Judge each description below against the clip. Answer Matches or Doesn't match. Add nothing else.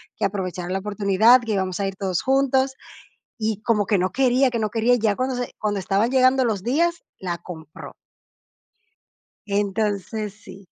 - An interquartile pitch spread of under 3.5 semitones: Doesn't match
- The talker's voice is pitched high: Matches